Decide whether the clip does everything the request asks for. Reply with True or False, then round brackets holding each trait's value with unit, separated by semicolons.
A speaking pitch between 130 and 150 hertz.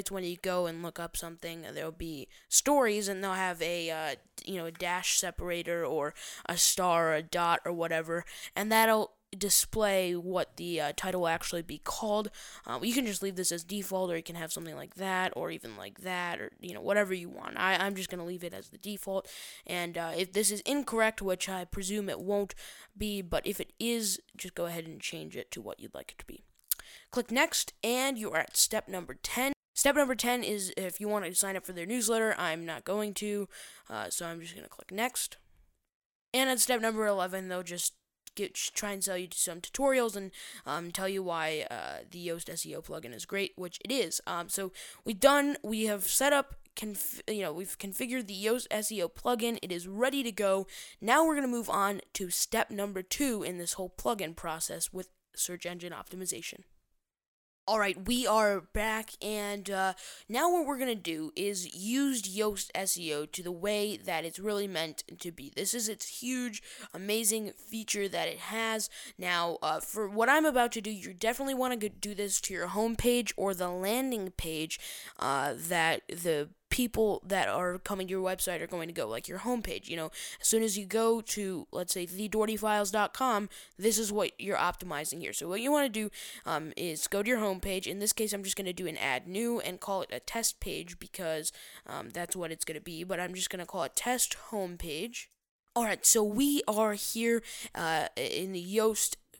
False (195 Hz)